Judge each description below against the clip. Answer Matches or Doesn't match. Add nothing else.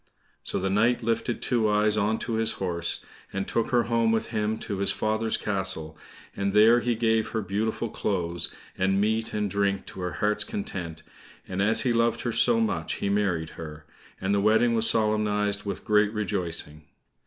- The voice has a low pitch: Matches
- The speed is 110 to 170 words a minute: Doesn't match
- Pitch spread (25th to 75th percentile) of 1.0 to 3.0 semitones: Matches